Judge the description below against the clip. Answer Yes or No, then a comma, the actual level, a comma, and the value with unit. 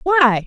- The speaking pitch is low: No, very high, 285 Hz